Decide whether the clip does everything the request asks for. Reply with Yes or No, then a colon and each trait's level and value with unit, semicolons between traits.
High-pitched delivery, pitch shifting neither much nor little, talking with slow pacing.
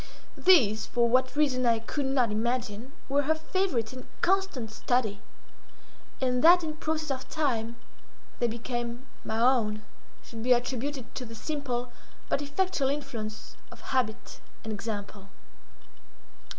Yes: very high, 250 Hz; average, 4.1 semitones; slow, 130 wpm